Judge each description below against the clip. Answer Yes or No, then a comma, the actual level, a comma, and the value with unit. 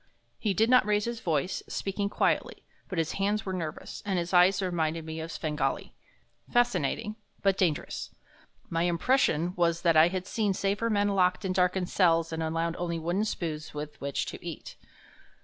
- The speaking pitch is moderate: Yes, medium, 180 Hz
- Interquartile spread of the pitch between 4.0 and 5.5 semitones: No, average, 3.5 semitones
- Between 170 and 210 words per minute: Yes, average, 175 wpm